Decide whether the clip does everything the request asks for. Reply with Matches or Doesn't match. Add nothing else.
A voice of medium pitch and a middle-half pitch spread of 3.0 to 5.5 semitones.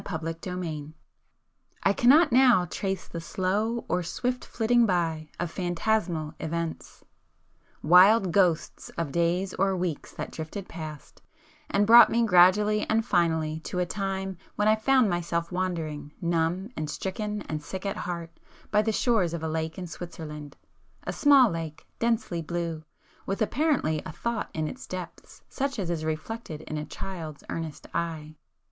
Matches